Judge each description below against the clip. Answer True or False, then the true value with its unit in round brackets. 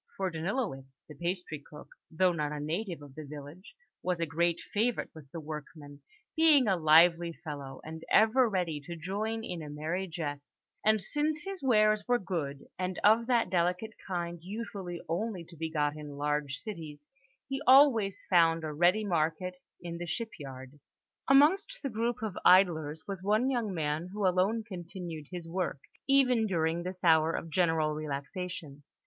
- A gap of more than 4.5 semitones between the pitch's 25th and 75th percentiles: True (5.4 semitones)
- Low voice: False (175 Hz)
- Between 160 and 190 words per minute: True (165 wpm)